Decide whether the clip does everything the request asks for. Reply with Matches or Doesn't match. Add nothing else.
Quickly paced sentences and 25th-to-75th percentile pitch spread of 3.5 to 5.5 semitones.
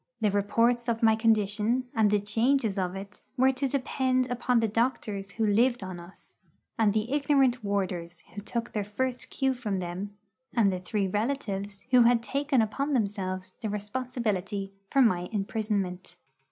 Doesn't match